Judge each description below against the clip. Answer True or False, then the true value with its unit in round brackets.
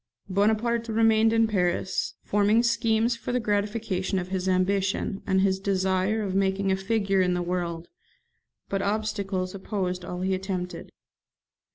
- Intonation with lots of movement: False (2.7 semitones)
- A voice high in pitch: True (195 Hz)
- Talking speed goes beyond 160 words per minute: False (145 wpm)